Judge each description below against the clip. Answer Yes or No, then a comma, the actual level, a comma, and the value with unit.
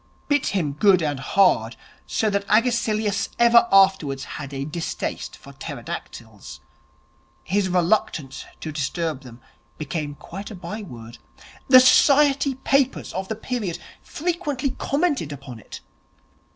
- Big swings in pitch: Yes, wide, 8.6 semitones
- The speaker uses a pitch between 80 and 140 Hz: No, high, 190 Hz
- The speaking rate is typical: No, slow, 125 wpm